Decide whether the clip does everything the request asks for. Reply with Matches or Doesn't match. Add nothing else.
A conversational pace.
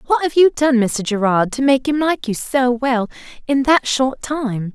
Doesn't match